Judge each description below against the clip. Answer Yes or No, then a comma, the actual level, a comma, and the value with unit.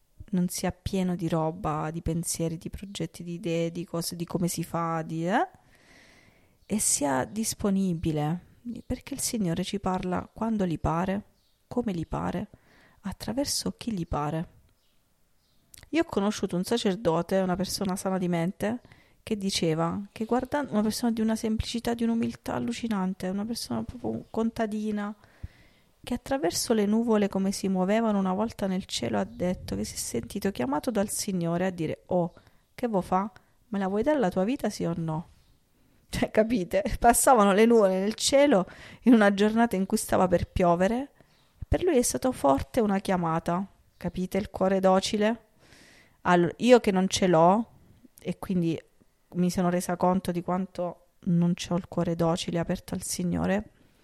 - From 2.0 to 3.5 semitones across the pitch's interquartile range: No, average, 4.2 semitones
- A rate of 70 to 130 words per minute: No, average, 165 wpm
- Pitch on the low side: No, high, 190 Hz